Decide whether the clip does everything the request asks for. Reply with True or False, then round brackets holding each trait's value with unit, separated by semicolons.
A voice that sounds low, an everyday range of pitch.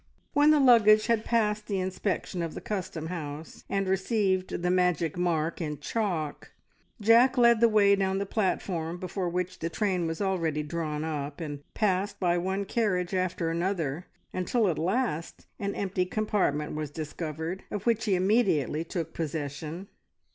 False (185 Hz; 4.0 semitones)